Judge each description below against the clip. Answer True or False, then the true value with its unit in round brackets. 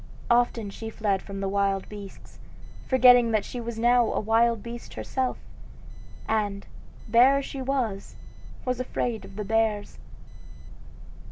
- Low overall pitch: False (225 Hz)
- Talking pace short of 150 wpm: True (140 wpm)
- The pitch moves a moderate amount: True (3.0 semitones)